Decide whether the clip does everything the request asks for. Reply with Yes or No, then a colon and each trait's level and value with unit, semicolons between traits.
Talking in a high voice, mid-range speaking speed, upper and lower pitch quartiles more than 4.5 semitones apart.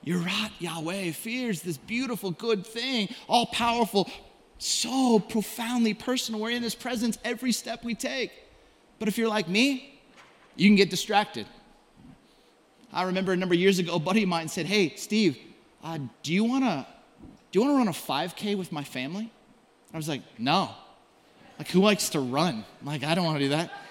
Yes: high, 210 Hz; average, 190 wpm; average, 5.1 semitones